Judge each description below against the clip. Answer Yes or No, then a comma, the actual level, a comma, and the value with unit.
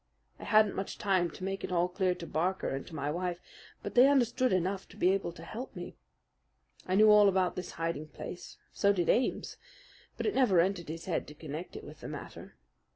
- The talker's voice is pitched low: No, medium, 185 Hz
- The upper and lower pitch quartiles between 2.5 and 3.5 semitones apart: Yes, average, 2.8 semitones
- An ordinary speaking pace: No, fast, 220 wpm